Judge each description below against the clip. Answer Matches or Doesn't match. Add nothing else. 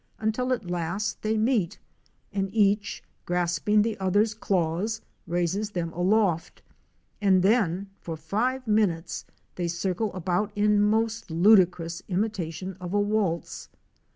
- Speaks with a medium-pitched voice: Doesn't match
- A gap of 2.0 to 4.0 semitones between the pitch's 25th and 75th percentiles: Matches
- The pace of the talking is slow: Matches